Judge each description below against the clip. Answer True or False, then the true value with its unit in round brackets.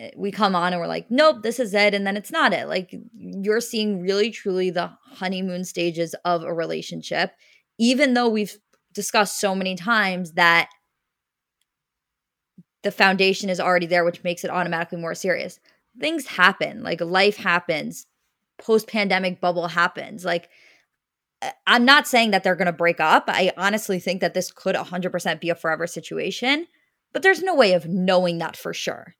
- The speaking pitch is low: False (185 Hz)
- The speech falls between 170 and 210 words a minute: True (175 wpm)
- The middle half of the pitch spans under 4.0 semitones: True (3.6 semitones)